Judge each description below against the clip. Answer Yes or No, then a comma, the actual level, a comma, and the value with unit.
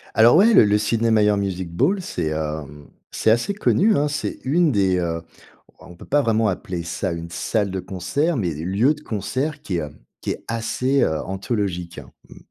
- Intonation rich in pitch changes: Yes, wide, 6.7 semitones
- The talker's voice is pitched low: Yes, low, 105 Hz